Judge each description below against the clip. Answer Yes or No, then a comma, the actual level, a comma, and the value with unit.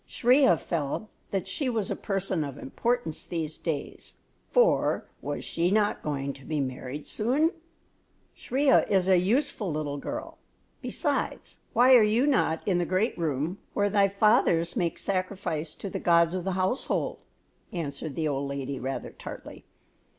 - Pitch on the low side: No, medium, 185 Hz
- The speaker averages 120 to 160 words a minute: Yes, average, 155 wpm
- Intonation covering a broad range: Yes, wide, 5.8 semitones